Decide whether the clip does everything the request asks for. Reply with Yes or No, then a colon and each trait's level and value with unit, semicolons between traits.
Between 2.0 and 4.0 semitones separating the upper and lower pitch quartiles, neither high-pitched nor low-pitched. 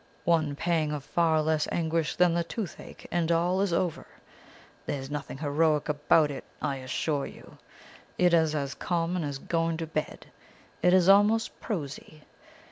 Yes: average, 2.7 semitones; medium, 160 Hz